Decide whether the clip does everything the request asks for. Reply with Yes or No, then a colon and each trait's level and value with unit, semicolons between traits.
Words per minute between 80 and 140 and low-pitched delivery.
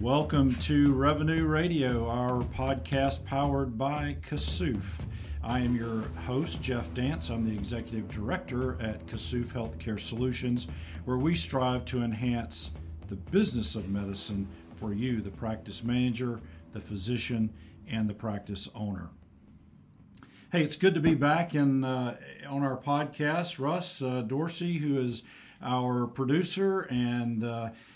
Yes: slow, 135 wpm; low, 120 Hz